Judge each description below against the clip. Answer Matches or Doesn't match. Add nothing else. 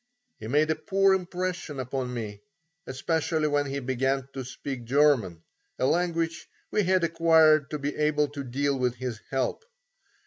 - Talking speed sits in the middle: Matches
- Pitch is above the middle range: Doesn't match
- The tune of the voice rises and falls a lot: Doesn't match